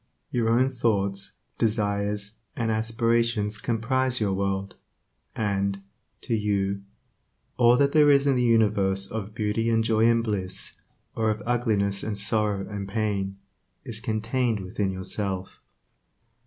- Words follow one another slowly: Yes, slow, 130 wpm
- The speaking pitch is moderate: No, low, 110 Hz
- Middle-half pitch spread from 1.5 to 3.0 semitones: Yes, average, 2.7 semitones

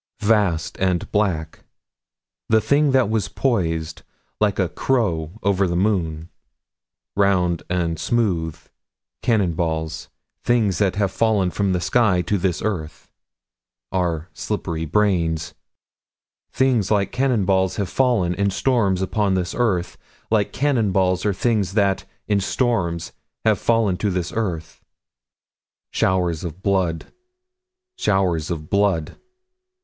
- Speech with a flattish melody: No, average, 3.6 semitones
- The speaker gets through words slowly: Yes, slow, 125 wpm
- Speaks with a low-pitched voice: Yes, very low, 95 Hz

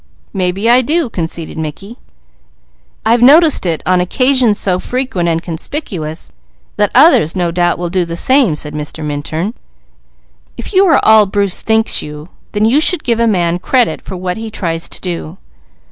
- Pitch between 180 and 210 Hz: Yes, medium, 185 Hz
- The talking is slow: No, average, 170 wpm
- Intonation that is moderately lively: No, wide, 5.7 semitones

